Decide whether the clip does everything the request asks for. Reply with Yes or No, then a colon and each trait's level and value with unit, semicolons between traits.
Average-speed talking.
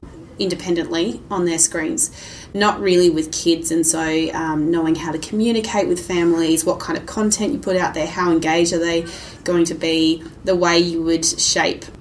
Yes: average, 185 wpm